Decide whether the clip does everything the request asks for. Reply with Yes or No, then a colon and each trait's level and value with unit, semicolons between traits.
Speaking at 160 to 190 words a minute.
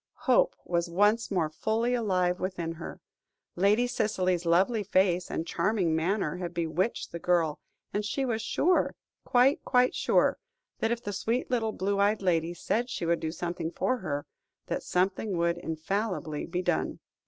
Yes: average, 165 wpm